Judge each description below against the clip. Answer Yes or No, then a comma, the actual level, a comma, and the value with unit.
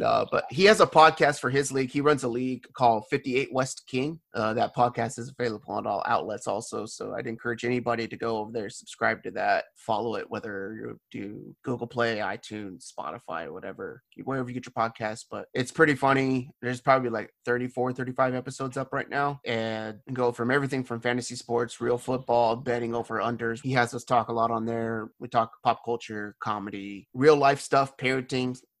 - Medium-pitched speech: No, low, 120 Hz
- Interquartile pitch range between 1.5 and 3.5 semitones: Yes, narrow, 2.4 semitones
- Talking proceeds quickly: No, average, 195 wpm